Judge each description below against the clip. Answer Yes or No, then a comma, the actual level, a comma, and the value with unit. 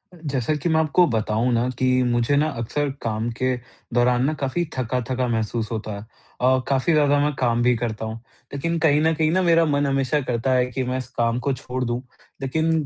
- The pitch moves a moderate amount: Yes, average, 3.8 semitones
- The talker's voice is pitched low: Yes, low, 130 Hz